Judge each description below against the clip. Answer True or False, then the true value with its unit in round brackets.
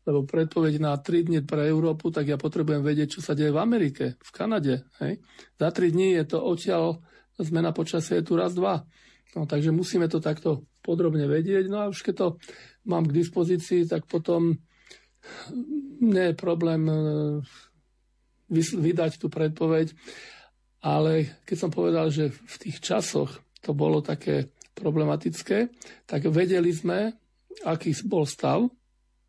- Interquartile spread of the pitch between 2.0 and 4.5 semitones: True (2.6 semitones)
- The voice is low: False (165 Hz)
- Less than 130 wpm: False (150 wpm)